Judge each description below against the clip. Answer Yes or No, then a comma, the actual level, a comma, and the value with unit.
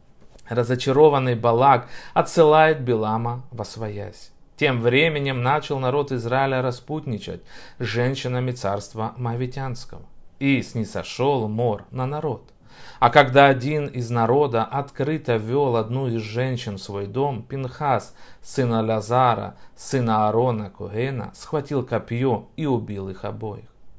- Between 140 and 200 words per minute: No, average, 115 wpm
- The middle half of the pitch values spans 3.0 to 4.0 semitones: Yes, average, 3.3 semitones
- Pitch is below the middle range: Yes, low, 125 Hz